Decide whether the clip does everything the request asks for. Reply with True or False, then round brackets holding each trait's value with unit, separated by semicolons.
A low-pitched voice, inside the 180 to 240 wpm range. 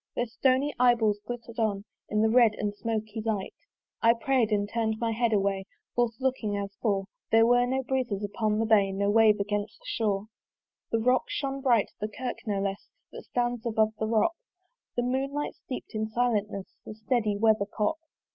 False (220 Hz; 185 wpm)